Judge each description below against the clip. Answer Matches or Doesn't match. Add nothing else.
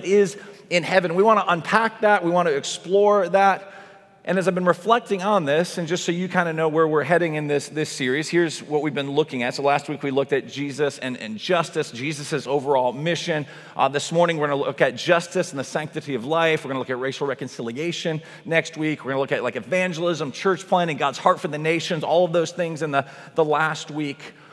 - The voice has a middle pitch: Matches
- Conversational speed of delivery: Doesn't match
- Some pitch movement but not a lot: Matches